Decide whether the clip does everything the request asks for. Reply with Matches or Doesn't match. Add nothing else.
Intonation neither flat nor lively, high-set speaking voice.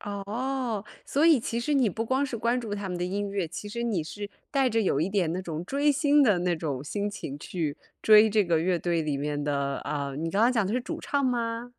Doesn't match